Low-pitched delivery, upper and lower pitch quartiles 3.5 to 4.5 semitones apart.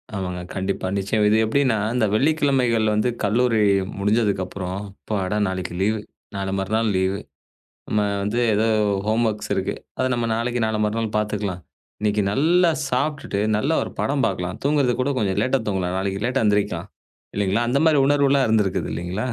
Yes: low, 110 Hz; average, 4.2 semitones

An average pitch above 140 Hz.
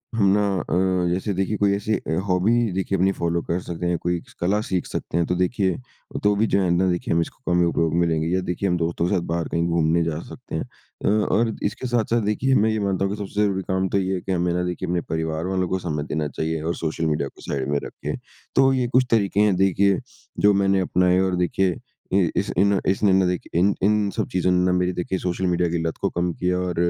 No: very low, 90 Hz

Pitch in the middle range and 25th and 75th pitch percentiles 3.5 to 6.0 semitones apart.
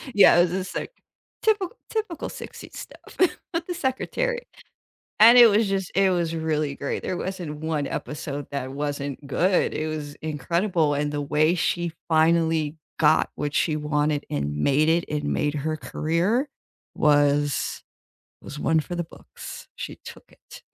Yes: medium, 160 Hz; average, 4.2 semitones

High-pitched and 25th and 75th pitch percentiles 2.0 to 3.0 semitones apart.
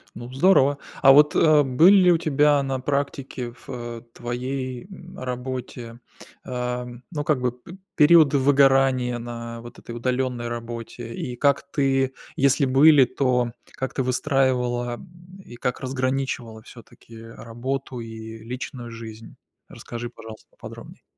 No: low, 130 Hz; narrow, 2.4 semitones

